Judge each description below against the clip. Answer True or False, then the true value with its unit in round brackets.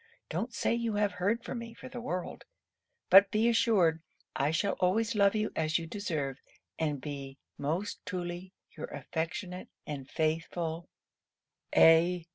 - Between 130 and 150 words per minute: True (145 wpm)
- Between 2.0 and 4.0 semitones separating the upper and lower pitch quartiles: False (4.7 semitones)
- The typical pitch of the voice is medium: True (180 Hz)